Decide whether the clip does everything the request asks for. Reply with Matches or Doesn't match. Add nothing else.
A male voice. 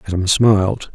Matches